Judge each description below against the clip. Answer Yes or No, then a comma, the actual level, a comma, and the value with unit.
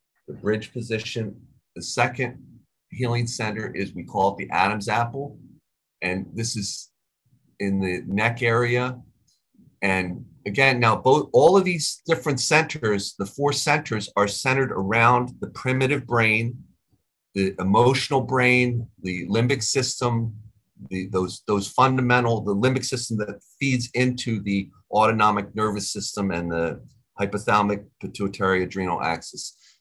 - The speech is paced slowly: Yes, slow, 130 wpm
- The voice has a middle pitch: No, low, 110 Hz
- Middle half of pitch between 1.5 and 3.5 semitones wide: No, average, 4.1 semitones